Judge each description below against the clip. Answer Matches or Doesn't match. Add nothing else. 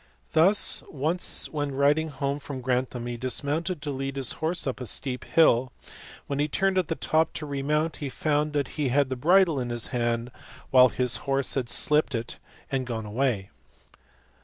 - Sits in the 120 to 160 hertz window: Matches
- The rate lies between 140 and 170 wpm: Doesn't match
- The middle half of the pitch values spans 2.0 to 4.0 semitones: Matches